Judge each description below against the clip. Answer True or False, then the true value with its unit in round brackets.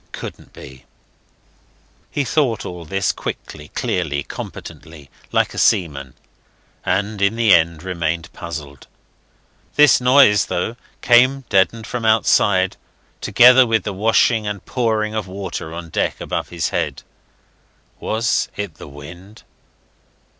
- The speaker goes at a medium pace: False (125 wpm)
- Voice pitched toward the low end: True (100 Hz)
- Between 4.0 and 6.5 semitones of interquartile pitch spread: True (5.2 semitones)